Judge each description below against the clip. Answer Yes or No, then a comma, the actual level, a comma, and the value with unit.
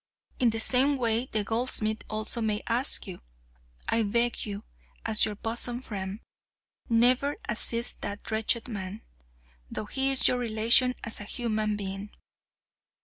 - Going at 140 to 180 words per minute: Yes, average, 145 wpm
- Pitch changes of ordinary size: No, narrow, 2.3 semitones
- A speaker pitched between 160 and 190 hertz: No, high, 225 Hz